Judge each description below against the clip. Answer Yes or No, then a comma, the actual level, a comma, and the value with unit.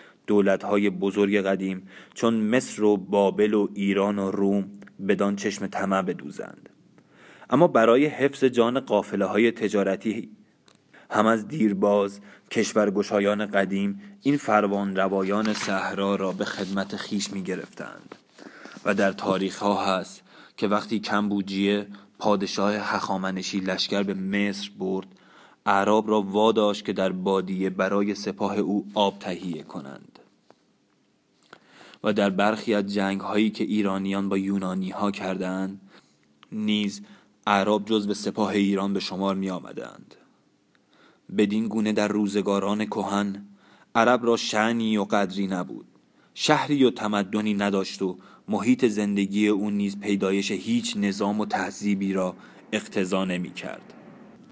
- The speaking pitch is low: Yes, low, 100 Hz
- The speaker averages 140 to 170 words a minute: No, average, 125 wpm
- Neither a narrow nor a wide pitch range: No, narrow, 1.5 semitones